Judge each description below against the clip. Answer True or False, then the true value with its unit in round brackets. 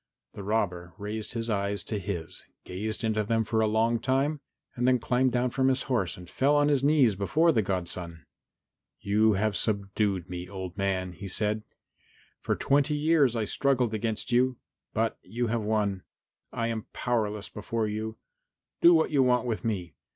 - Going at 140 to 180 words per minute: True (175 wpm)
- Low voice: True (110 Hz)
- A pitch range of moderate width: True (3.8 semitones)